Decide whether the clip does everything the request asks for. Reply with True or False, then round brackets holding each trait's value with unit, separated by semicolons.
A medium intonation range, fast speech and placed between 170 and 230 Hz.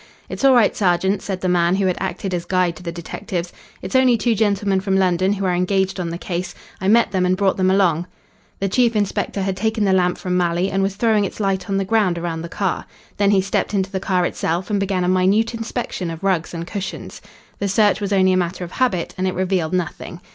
False (2.0 semitones; 240 wpm; 190 Hz)